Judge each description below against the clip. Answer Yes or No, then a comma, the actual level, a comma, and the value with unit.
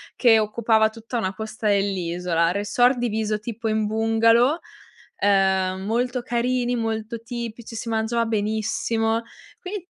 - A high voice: Yes, high, 225 Hz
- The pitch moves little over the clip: Yes, narrow, 2.1 semitones